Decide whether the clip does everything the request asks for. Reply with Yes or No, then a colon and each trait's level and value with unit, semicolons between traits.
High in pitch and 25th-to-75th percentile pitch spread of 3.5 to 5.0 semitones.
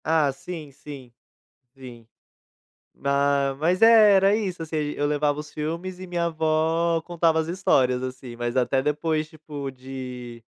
No: medium, 150 Hz; average, 3.8 semitones